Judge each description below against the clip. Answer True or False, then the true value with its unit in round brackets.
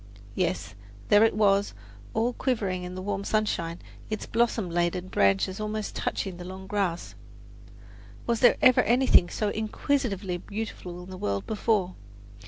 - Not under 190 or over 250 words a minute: False (145 wpm)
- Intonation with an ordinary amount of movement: True (3.4 semitones)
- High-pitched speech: True (200 Hz)